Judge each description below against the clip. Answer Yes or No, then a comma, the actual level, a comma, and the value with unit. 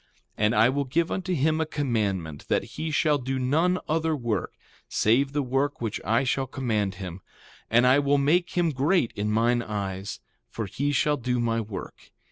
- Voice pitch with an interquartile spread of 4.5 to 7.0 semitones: Yes, average, 5.1 semitones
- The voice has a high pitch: No, low, 130 Hz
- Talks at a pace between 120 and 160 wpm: No, average, 190 wpm